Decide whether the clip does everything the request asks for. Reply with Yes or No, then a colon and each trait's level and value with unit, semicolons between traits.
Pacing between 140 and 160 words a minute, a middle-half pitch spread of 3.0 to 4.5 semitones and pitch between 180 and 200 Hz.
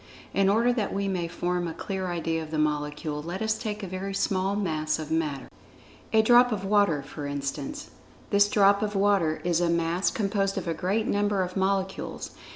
No: average, 195 wpm; average, 3.9 semitones; high, 190 Hz